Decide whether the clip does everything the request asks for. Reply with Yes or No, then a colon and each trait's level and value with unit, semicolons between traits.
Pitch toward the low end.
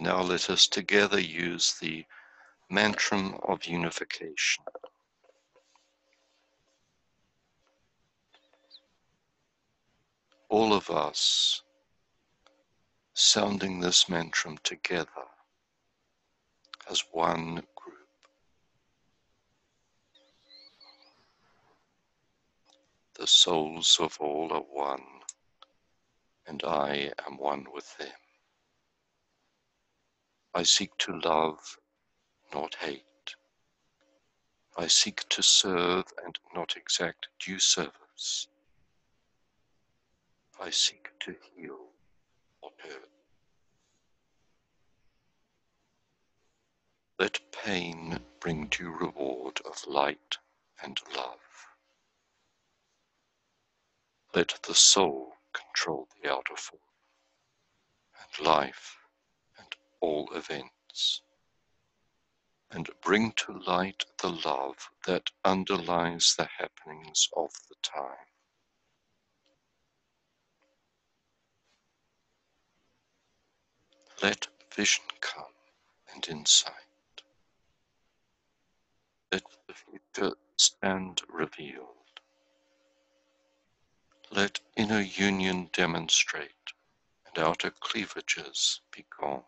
Yes: very low, 80 Hz